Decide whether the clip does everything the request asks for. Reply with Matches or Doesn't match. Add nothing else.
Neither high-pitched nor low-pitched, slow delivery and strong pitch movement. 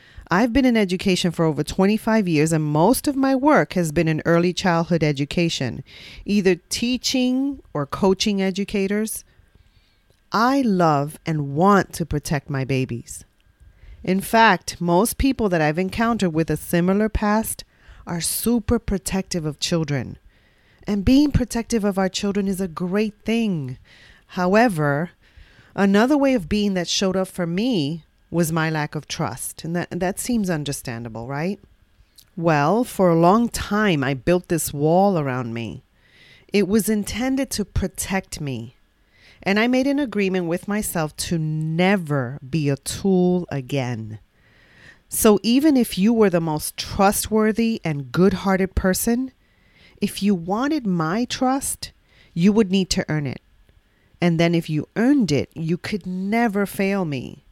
Doesn't match